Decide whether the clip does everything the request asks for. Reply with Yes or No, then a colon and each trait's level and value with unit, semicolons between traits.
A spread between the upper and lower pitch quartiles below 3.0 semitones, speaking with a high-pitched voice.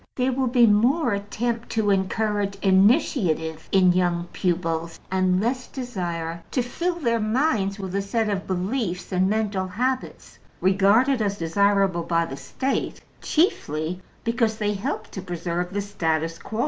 No: average, 4.4 semitones; high, 200 Hz